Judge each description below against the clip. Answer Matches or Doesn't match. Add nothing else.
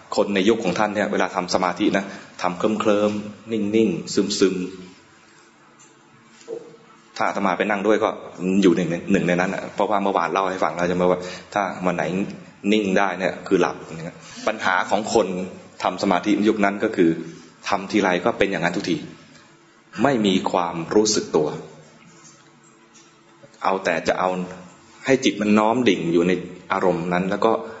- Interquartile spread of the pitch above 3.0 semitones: Doesn't match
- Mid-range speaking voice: Doesn't match